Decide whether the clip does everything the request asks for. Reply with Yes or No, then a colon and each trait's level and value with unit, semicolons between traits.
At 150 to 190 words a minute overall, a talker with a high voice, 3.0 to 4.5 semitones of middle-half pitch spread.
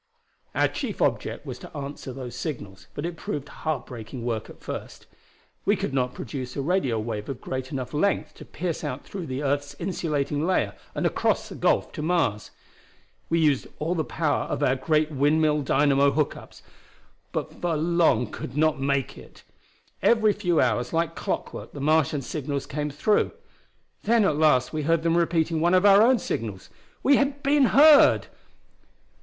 No: average, 170 wpm; medium, 150 Hz; average, 4.1 semitones